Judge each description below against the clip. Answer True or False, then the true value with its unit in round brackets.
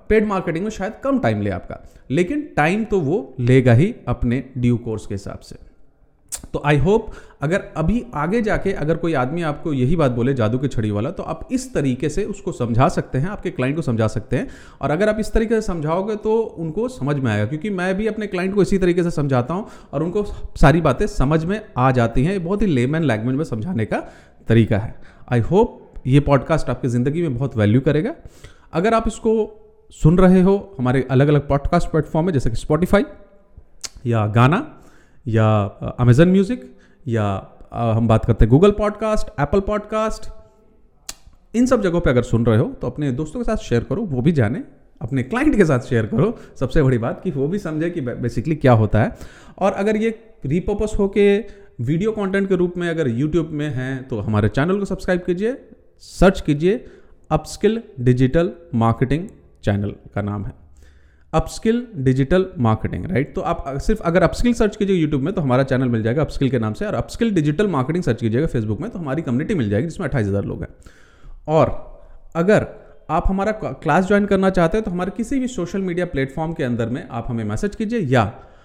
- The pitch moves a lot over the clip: True (8.0 semitones)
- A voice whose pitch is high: False (155 Hz)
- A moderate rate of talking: False (200 wpm)